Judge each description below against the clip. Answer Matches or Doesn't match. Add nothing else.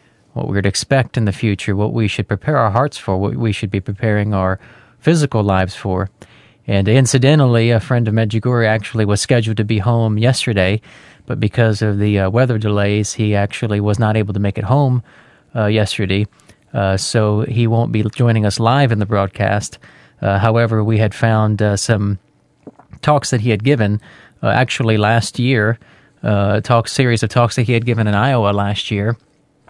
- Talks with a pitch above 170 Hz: Doesn't match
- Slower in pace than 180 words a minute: Doesn't match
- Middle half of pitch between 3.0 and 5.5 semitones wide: Doesn't match